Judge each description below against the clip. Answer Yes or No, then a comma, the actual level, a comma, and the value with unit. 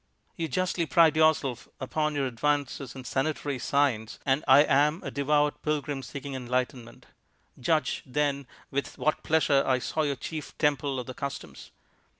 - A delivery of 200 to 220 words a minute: No, average, 155 wpm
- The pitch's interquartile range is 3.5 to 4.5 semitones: No, narrow, 2.5 semitones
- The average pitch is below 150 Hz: Yes, medium, 140 Hz